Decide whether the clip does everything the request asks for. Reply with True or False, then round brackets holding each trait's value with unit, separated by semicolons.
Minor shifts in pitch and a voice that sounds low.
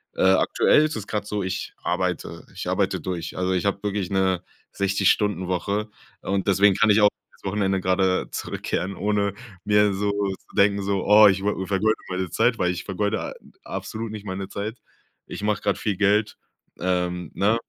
True (1.9 semitones; 100 Hz)